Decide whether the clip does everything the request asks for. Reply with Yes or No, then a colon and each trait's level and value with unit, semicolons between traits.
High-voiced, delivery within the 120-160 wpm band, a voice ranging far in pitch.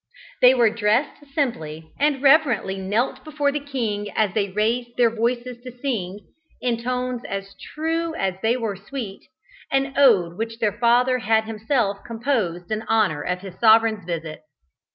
No: high, 230 Hz; average, 155 wpm; average, 4.0 semitones